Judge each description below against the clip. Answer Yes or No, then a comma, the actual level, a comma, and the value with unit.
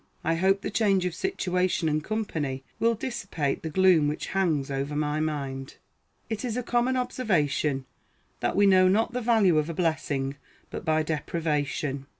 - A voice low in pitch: No, medium, 165 Hz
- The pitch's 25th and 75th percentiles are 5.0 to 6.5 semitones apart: Yes, wide, 5.6 semitones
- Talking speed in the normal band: Yes, average, 165 wpm